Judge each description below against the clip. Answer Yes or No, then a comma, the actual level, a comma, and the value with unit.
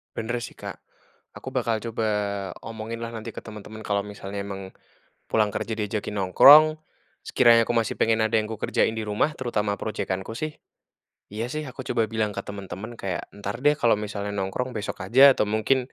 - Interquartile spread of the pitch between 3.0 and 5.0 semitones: No, narrow, 2.4 semitones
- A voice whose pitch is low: Yes, low, 110 Hz